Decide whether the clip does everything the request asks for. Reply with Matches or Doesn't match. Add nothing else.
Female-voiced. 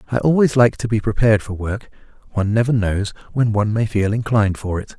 Doesn't match